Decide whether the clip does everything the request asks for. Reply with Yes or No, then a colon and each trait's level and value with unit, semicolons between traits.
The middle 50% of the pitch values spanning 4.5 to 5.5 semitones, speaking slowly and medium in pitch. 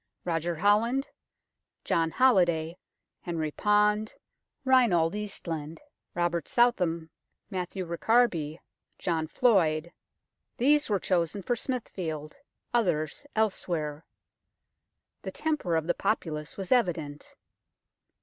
Yes: average, 5.1 semitones; slow, 90 wpm; medium, 175 Hz